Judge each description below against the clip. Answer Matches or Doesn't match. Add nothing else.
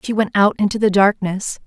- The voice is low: Doesn't match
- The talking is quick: Matches